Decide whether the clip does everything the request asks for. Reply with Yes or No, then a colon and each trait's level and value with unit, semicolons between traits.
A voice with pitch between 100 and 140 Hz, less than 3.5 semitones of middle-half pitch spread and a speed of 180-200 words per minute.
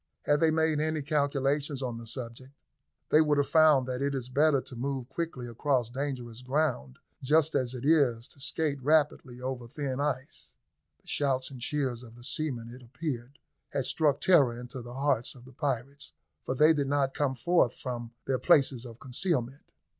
Yes: low, 135 Hz; average, 3.0 semitones; average, 185 wpm